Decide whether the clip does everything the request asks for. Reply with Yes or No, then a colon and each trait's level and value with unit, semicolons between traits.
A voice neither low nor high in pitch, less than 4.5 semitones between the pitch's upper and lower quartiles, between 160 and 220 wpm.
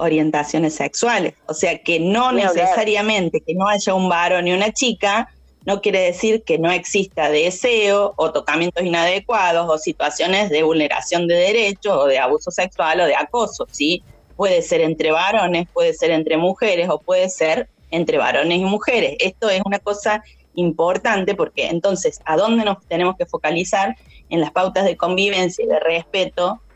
Yes: medium, 180 Hz; average, 3.8 semitones; average, 170 wpm